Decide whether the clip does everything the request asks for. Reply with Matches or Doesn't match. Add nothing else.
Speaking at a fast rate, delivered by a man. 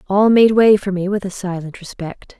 Doesn't match